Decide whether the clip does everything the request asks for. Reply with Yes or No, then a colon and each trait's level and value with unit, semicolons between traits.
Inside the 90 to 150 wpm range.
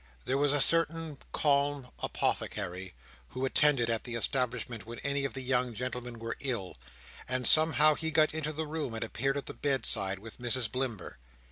No: average, 175 wpm